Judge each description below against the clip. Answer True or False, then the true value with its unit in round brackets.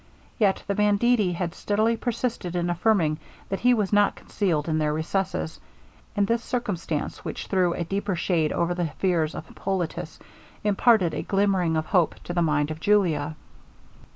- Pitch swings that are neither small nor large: True (4.0 semitones)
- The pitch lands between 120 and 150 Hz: False (185 Hz)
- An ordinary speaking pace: True (165 wpm)